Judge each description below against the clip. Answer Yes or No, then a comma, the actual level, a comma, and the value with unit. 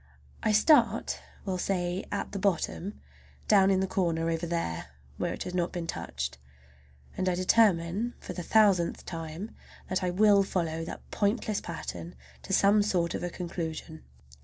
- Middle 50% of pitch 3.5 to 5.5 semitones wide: No, average, 3.1 semitones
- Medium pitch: Yes, medium, 180 Hz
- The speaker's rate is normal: Yes, average, 160 wpm